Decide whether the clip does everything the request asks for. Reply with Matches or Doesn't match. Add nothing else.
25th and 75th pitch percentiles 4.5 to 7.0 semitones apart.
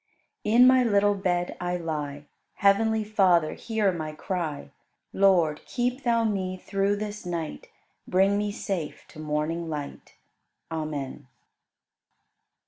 Matches